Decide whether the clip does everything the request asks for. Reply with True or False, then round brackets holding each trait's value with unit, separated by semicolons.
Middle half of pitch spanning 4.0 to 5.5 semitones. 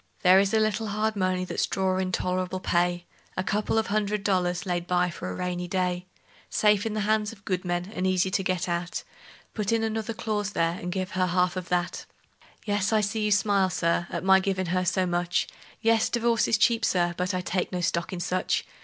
False (2.6 semitones)